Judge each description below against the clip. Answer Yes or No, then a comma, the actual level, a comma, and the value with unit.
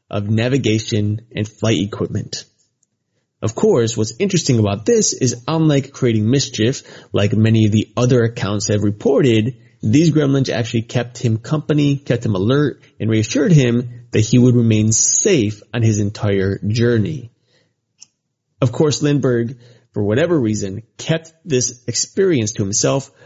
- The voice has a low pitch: Yes, low, 120 Hz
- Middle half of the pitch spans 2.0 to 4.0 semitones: Yes, average, 3.7 semitones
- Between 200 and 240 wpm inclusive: No, average, 140 wpm